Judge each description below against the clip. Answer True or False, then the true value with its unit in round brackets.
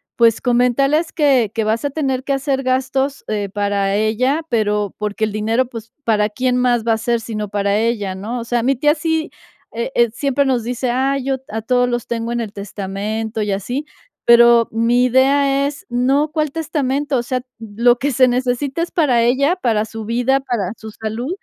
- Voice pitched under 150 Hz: False (240 Hz)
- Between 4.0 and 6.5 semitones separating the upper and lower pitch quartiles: False (3.5 semitones)